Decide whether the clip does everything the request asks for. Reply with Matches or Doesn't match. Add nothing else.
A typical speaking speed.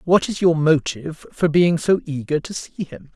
Doesn't match